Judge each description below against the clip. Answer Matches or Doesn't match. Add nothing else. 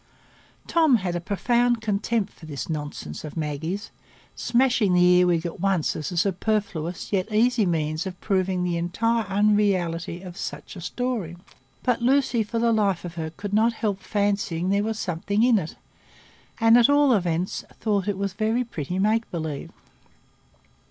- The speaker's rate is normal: Matches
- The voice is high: Matches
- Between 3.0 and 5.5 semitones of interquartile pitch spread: Matches